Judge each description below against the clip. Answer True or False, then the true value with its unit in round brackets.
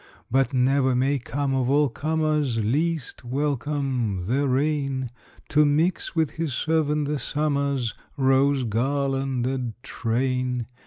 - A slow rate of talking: True (115 wpm)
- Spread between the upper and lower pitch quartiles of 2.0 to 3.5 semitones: True (2.5 semitones)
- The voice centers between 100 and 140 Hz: True (135 Hz)